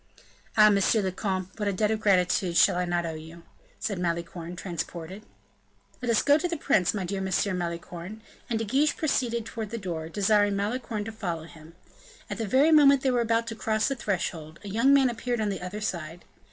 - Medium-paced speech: No, fast, 210 wpm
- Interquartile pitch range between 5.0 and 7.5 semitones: No, average, 4.5 semitones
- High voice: Yes, high, 205 Hz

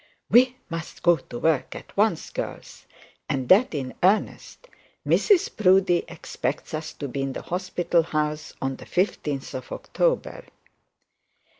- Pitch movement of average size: Yes, average, 4.8 semitones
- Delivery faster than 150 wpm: No, average, 140 wpm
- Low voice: No, medium, 165 Hz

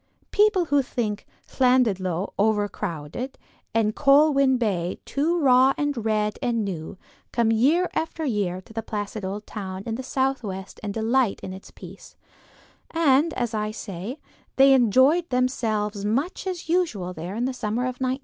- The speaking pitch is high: Yes, high, 230 Hz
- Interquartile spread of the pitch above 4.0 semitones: Yes, average, 4.6 semitones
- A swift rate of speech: No, average, 155 wpm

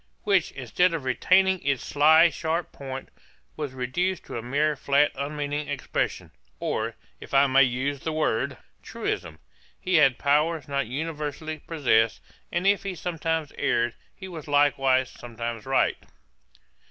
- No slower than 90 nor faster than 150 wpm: Yes, average, 140 wpm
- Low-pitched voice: No, medium, 145 Hz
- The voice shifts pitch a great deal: No, average, 3.5 semitones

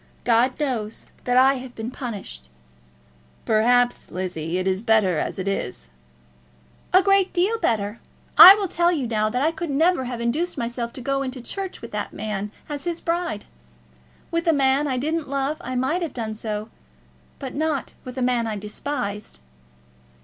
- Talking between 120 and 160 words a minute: No, average, 170 wpm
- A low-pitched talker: No, very high, 250 Hz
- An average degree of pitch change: No, wide, 5.7 semitones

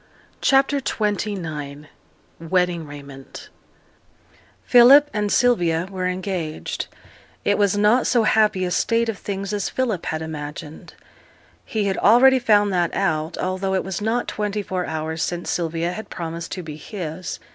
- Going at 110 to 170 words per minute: Yes, average, 145 wpm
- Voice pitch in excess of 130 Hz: Yes, high, 190 Hz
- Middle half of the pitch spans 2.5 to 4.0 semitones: No, average, 4.4 semitones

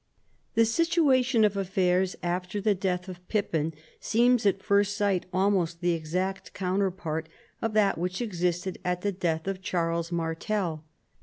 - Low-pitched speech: No, medium, 185 Hz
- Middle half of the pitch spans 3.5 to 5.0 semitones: No, average, 2.8 semitones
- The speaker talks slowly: No, average, 145 wpm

